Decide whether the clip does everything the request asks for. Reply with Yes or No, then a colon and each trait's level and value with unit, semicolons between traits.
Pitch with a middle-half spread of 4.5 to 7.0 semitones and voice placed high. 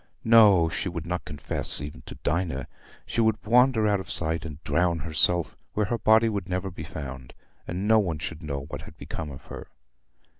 No: average, 5.2 semitones; very low, 85 Hz